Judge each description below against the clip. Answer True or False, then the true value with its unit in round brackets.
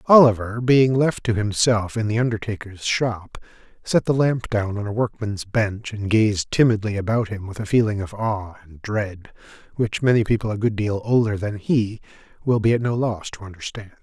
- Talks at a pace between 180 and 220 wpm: True (190 wpm)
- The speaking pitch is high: False (110 Hz)